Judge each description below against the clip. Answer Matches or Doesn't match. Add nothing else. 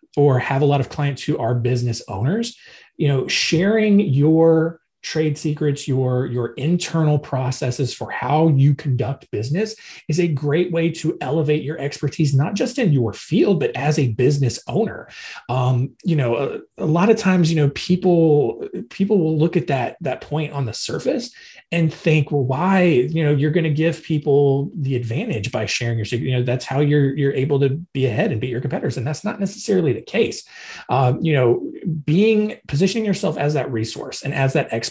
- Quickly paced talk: Doesn't match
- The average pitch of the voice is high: Doesn't match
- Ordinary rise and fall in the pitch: Matches